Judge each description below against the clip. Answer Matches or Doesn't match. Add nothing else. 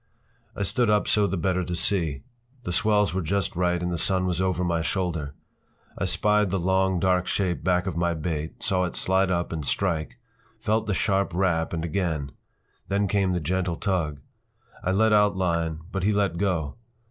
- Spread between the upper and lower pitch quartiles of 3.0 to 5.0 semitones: Doesn't match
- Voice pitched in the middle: Doesn't match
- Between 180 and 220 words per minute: Matches